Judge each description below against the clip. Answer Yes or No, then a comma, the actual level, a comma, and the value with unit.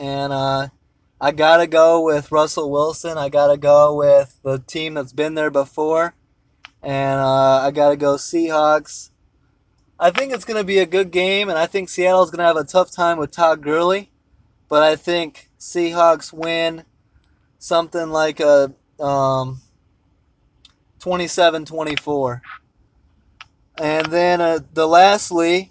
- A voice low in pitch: No, medium, 155 Hz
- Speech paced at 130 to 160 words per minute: Yes, average, 140 wpm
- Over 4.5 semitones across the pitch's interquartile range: No, average, 3.6 semitones